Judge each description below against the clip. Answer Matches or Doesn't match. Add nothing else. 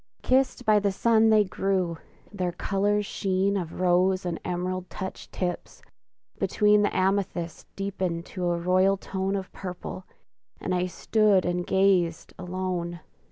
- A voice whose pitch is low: Doesn't match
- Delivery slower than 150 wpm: Matches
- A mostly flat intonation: Matches